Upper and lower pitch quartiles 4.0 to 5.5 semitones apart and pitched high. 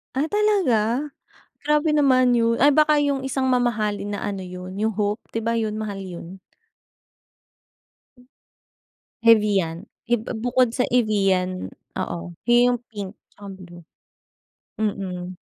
Yes: average, 4.5 semitones; high, 220 Hz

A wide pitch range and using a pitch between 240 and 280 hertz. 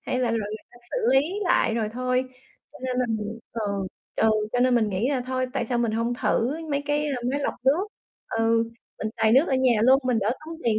No: average, 2.8 semitones; high, 245 Hz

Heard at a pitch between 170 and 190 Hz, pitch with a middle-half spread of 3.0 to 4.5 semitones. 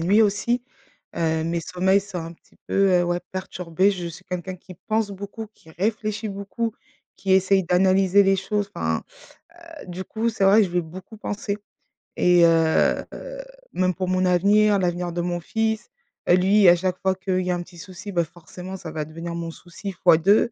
No: medium, 185 Hz; narrow, 2.5 semitones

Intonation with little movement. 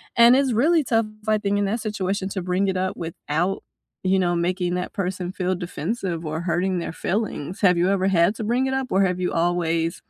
No: average, 3.0 semitones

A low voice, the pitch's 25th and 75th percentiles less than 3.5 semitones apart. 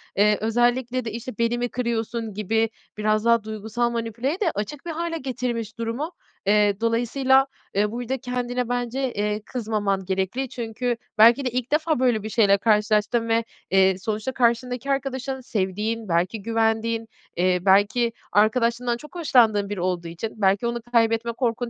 No: high, 230 Hz; average, 2.8 semitones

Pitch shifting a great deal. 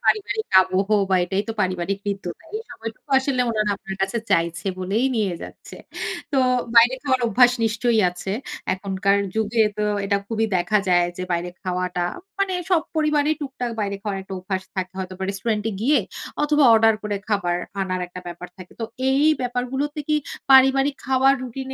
Yes: wide, 5.7 semitones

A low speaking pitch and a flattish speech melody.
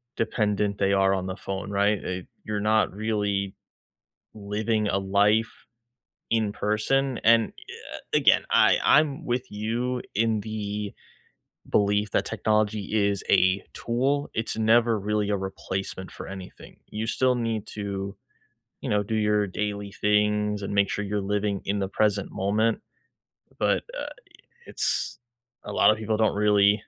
Yes: low, 105 Hz; narrow, 1.6 semitones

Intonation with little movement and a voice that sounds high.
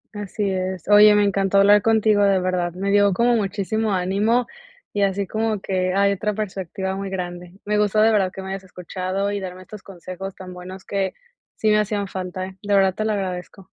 Yes: narrow, 1.9 semitones; high, 195 Hz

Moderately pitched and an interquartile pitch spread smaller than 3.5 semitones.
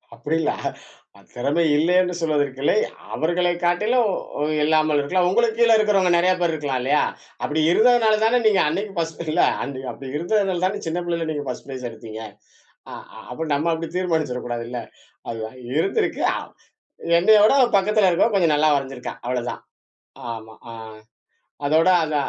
No: medium, 165 Hz; average, 4.9 semitones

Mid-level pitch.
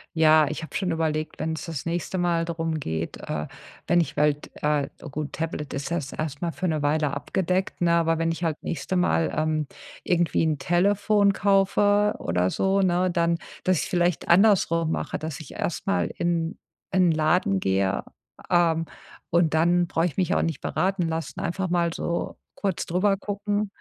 Yes: medium, 165 Hz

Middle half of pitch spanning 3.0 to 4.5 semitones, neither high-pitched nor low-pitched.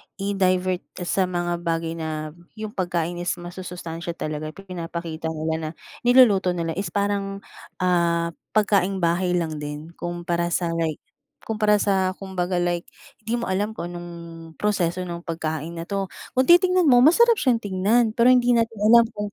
Yes: average, 3.5 semitones; medium, 180 Hz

